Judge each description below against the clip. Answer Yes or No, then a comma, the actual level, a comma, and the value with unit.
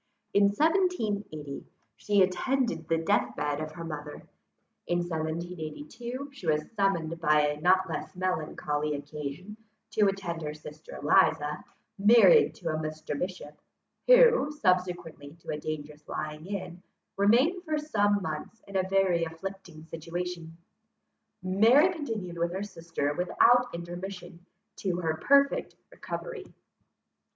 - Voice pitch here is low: No, medium, 175 Hz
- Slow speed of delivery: Yes, slow, 125 wpm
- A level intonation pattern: No, average, 4.8 semitones